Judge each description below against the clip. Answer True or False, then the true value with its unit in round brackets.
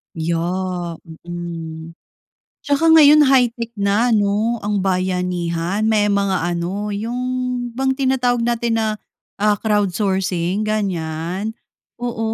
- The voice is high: True (205 Hz)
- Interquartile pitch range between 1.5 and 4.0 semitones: False (4.8 semitones)